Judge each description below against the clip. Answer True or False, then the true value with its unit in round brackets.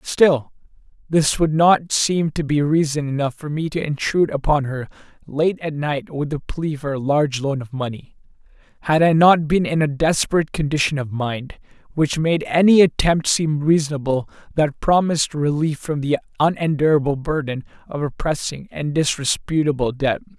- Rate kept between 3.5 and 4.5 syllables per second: False (5.0 syllables/s)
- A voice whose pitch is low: False (150 Hz)